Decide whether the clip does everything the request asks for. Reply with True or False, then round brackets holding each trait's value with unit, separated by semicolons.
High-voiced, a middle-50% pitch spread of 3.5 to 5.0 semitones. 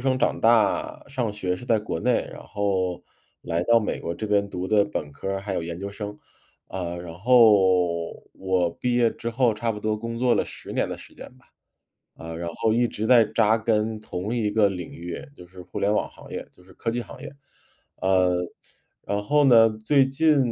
False (105 Hz; 4.0 semitones)